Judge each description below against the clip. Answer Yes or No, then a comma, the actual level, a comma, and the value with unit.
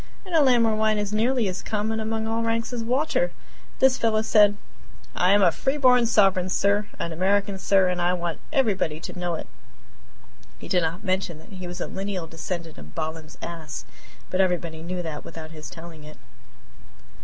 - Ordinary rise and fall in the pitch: Yes, average, 4.7 semitones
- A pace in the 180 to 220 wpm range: Yes, average, 190 wpm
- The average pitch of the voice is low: No, high, 190 Hz